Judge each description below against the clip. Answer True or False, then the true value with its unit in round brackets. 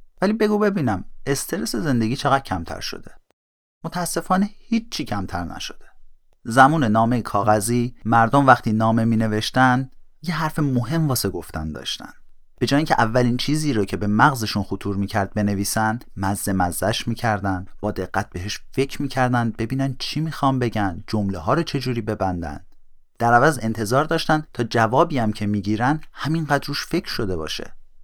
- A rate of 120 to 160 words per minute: True (150 wpm)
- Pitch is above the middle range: False (120 Hz)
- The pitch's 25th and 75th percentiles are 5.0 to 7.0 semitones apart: True (5.6 semitones)